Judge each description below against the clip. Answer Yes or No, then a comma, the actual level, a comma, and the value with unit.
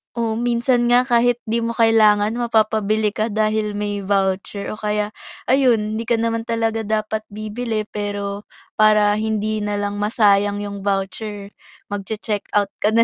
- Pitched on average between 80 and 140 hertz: No, high, 215 Hz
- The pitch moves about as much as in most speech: No, narrow, 1.7 semitones